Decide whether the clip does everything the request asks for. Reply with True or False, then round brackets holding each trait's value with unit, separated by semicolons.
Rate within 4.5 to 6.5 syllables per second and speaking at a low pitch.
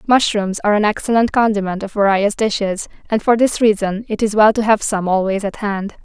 False (5.5 syllables/s; 210 Hz)